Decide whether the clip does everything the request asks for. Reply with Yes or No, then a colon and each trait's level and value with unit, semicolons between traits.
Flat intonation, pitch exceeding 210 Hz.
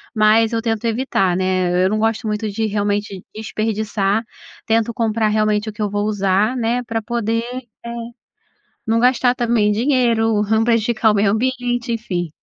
Yes: narrow, 1.9 semitones; high, 220 Hz